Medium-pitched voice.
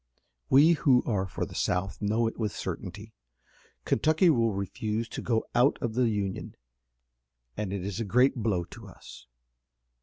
No: low, 110 Hz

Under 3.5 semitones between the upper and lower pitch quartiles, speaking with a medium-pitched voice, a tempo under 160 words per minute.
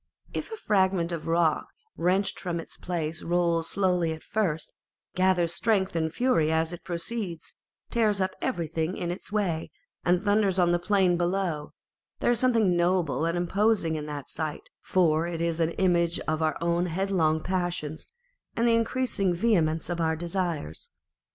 No: average, 2.8 semitones; medium, 175 Hz; average, 165 wpm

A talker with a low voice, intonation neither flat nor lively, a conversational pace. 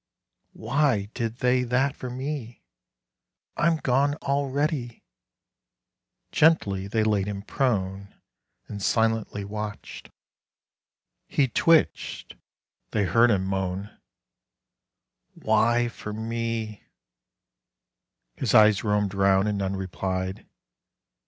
No: low, 110 Hz; average, 4.1 semitones; slow, 95 wpm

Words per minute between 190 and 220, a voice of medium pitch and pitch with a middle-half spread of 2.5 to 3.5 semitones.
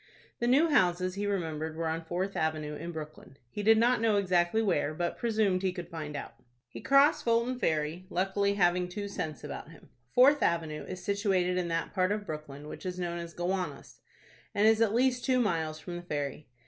No: average, 200 wpm; medium, 180 Hz; average, 4.5 semitones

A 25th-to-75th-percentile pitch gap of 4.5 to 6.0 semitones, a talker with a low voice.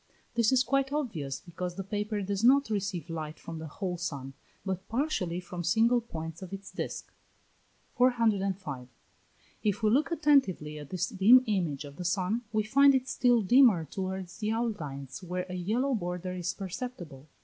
No: average, 5.2 semitones; high, 190 Hz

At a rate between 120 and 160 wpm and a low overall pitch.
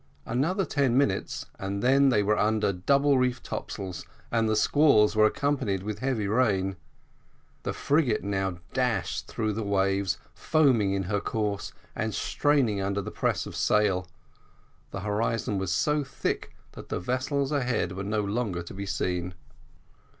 Yes: average, 155 wpm; low, 105 Hz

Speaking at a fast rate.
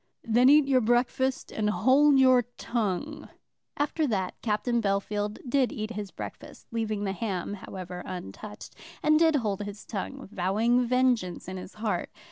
No: average, 150 wpm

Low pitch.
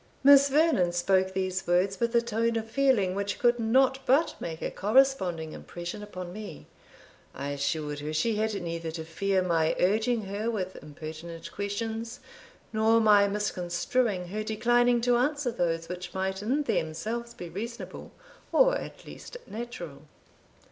No: high, 205 Hz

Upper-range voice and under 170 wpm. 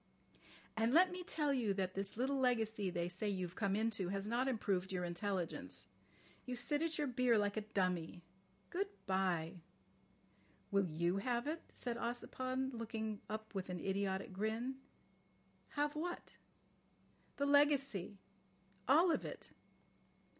Yes: high, 220 Hz; average, 140 wpm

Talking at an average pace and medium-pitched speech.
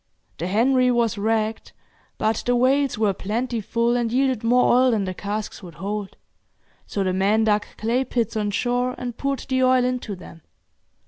No: average, 175 wpm; high, 230 Hz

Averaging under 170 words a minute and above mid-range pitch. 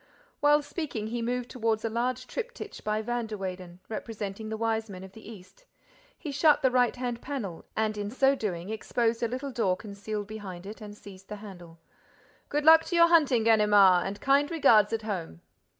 No: average, 195 wpm; high, 220 Hz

